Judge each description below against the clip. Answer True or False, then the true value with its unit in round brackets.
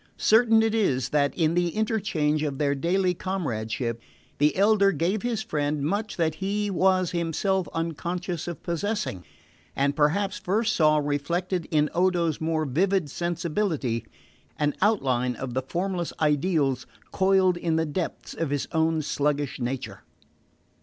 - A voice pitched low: False (165 Hz)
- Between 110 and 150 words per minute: True (140 wpm)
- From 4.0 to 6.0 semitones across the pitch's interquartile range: True (4.6 semitones)